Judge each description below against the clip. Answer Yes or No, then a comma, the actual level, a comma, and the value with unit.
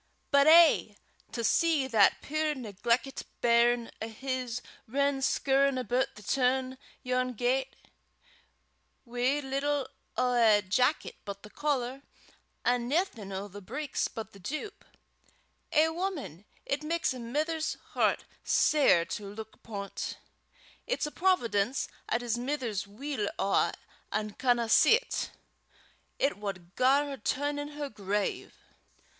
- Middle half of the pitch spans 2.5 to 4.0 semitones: No, average, 4.7 semitones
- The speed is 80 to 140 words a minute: Yes, slow, 135 wpm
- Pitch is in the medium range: No, very high, 255 Hz